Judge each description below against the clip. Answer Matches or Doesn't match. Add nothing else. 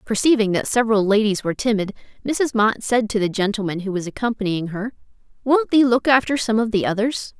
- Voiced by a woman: Matches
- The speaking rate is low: Doesn't match